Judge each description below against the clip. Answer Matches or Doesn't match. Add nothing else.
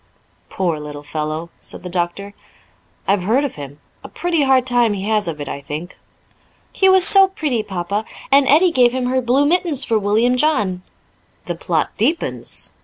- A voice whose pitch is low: Doesn't match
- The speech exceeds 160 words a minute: Matches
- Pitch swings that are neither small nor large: Doesn't match